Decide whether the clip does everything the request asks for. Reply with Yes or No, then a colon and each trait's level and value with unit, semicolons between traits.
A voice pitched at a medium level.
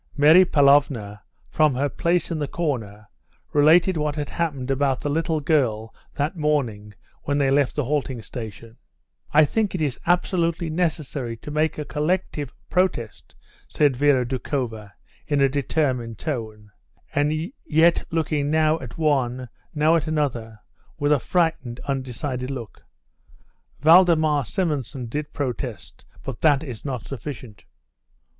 Yes: medium, 145 Hz